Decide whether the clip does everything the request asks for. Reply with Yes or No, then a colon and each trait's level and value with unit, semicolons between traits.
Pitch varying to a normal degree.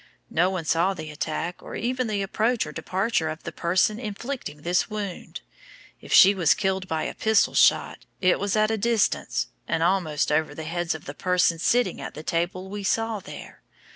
Yes: average, 4.4 semitones